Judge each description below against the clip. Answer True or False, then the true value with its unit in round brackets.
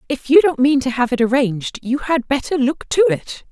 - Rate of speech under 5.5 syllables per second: True (5.3 syllables/s)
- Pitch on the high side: True (265 Hz)